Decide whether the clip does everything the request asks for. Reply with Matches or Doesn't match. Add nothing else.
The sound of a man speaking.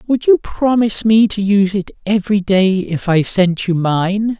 Matches